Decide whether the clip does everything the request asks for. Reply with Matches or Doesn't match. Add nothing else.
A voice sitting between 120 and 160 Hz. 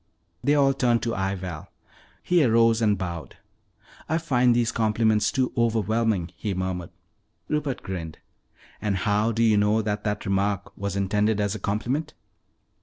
Doesn't match